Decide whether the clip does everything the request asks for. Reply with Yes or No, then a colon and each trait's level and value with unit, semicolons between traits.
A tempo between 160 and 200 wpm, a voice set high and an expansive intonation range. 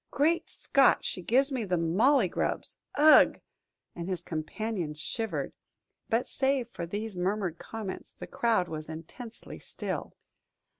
No: slow, 135 wpm; high, 210 Hz; wide, 6.2 semitones